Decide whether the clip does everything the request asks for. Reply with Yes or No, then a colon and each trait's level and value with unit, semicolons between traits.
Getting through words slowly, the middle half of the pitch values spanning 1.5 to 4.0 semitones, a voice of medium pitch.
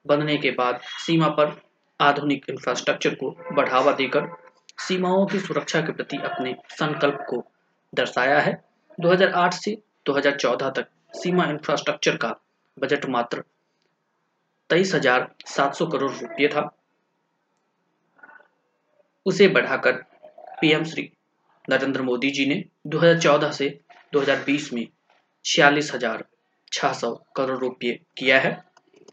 No: slow, 105 wpm; average, 4.6 semitones; medium, 150 Hz